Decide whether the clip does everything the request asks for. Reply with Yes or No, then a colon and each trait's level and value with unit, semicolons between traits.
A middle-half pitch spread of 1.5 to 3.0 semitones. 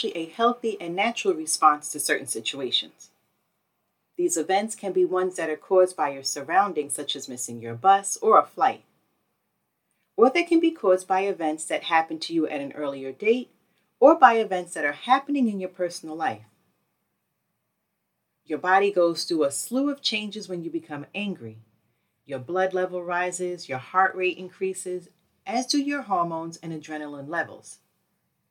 No: average, 4.6 semitones